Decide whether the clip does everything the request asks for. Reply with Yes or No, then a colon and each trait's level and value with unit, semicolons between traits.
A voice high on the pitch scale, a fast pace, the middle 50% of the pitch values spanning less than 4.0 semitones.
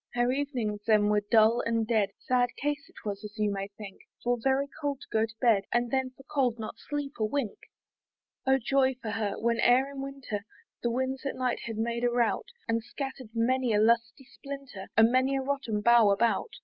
Yes: high, 240 Hz; fast, 210 wpm; average, 3.4 semitones